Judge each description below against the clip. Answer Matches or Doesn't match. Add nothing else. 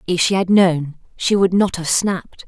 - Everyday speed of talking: Doesn't match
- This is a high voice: Doesn't match